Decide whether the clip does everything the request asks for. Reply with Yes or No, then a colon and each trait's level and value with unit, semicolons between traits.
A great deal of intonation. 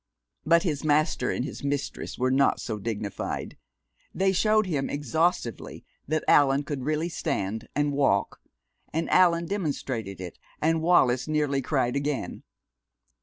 No: average, 4.2 semitones